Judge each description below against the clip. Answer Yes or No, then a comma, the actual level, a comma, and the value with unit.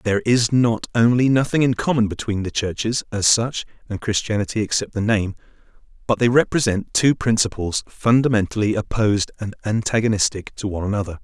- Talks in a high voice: No, low, 110 Hz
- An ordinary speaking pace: Yes, average, 155 wpm